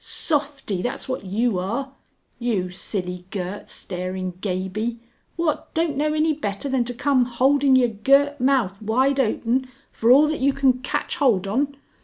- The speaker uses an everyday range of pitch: No, wide, 5.7 semitones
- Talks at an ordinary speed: Yes, average, 165 wpm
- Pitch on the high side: Yes, high, 245 Hz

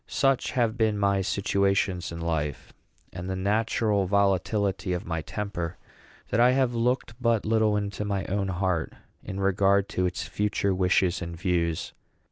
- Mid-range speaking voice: No, low, 100 Hz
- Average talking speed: Yes, average, 155 wpm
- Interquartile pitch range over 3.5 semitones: No, average, 2.7 semitones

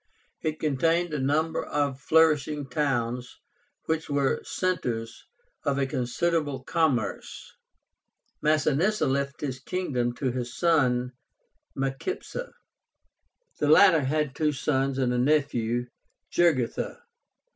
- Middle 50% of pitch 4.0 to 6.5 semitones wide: No, average, 3.5 semitones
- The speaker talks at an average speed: No, slow, 105 wpm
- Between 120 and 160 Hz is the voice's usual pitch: Yes, medium, 140 Hz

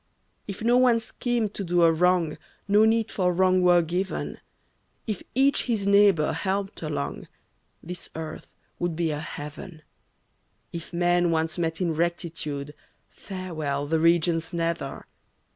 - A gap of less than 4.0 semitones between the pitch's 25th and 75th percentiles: Yes, average, 3.3 semitones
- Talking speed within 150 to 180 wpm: No, average, 140 wpm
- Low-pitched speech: No, medium, 175 Hz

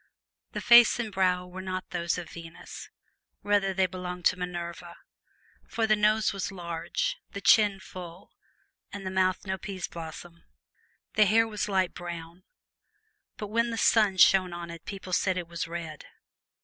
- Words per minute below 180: Yes, average, 160 wpm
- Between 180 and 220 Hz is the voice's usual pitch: Yes, medium, 185 Hz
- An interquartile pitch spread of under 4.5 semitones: Yes, average, 2.9 semitones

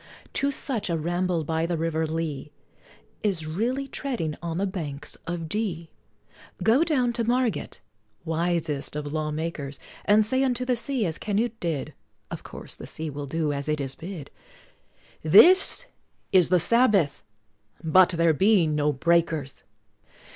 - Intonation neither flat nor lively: No, wide, 5.9 semitones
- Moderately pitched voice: Yes, medium, 170 Hz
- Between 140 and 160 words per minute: Yes, average, 155 wpm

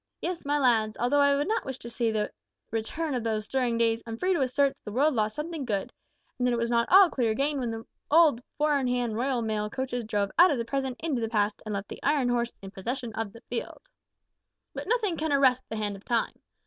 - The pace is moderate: No, fast, 250 wpm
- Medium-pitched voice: No, high, 245 Hz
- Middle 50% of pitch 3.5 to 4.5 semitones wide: Yes, average, 4.1 semitones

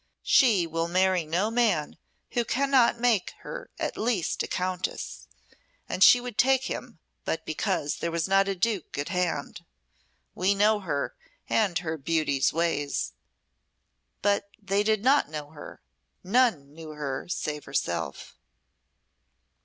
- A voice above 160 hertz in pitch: Yes, medium, 185 Hz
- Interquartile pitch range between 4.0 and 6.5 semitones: Yes, wide, 5.6 semitones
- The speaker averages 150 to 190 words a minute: No, slow, 135 wpm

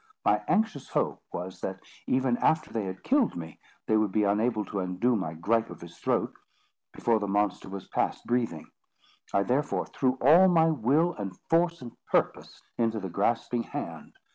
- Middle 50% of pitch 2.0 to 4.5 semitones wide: No, wide, 5.6 semitones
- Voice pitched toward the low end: Yes, low, 115 Hz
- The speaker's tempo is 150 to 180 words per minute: Yes, average, 175 wpm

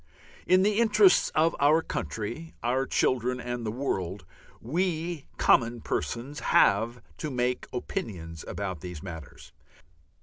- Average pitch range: No, wide, 7.2 semitones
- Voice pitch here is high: No, low, 125 Hz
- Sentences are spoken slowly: Yes, slow, 125 wpm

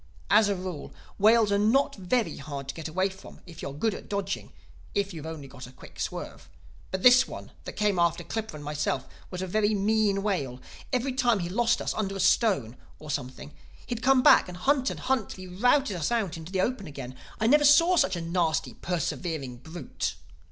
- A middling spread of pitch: No, wide, 5.7 semitones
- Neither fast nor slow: No, fast, 210 wpm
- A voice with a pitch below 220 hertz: Yes, high, 190 Hz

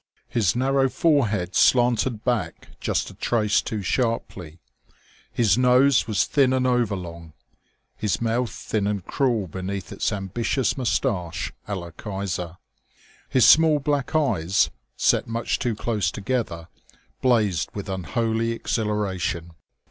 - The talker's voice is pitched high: No, low, 110 Hz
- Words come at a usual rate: No, slow, 125 wpm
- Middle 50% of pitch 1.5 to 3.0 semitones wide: No, average, 4.8 semitones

